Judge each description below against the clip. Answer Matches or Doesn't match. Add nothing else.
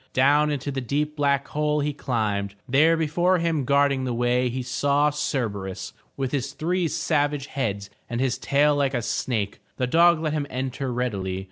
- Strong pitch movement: Doesn't match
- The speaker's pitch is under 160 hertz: Matches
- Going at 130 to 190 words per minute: Matches